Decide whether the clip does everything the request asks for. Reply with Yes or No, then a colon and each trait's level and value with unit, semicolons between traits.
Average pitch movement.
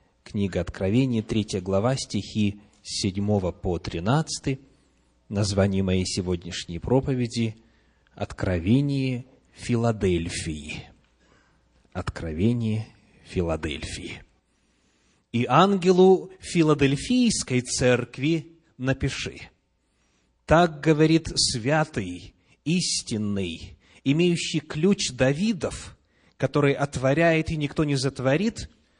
No: wide, 7.3 semitones